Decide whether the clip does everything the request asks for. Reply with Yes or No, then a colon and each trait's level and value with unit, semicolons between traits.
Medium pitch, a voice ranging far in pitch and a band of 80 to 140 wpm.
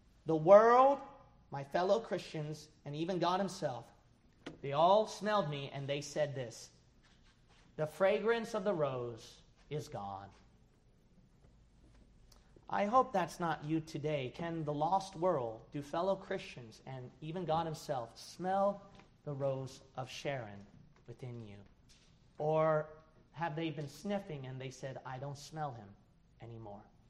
Yes: medium, 150 Hz; wide, 6.0 semitones; slow, 135 wpm